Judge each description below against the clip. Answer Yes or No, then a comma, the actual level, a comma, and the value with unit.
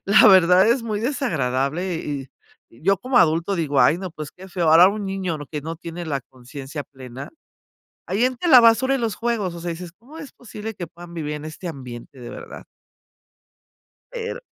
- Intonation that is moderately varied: No, wide, 6.4 semitones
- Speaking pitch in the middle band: Yes, medium, 175 Hz